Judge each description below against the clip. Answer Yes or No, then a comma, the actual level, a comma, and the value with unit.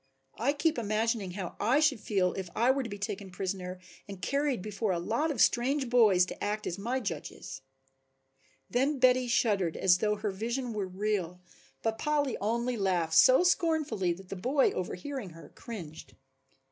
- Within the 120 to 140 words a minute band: No, average, 170 wpm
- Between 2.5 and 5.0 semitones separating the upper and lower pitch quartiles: No, wide, 5.4 semitones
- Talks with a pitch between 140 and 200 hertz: No, high, 215 Hz